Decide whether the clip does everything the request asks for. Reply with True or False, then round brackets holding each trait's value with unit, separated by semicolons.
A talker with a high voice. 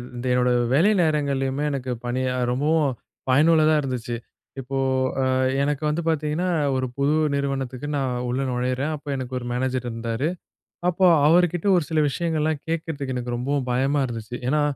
False (140 Hz)